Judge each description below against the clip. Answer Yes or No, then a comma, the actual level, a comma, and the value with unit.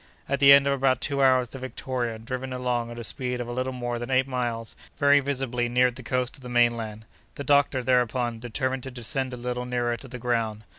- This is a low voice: Yes, low, 125 Hz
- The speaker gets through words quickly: Yes, fast, 230 wpm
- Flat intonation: Yes, narrow, 1.6 semitones